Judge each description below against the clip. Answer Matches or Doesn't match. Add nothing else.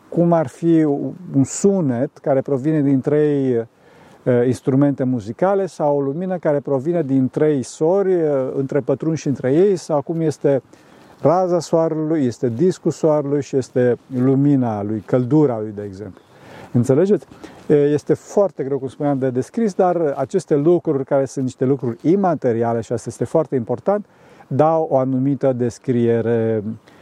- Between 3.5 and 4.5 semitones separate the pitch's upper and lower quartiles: Matches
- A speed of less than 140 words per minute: Doesn't match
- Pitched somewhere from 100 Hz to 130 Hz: Doesn't match